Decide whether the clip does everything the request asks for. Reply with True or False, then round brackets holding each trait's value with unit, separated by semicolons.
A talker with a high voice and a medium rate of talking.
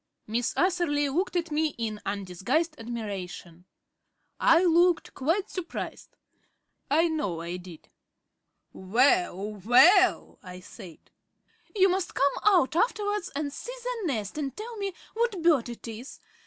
False (290 Hz; 130 wpm)